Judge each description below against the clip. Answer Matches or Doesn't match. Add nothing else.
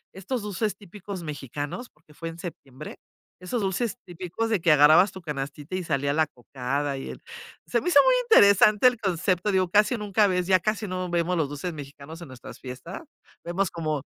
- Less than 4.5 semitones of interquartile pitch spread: Doesn't match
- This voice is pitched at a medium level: Matches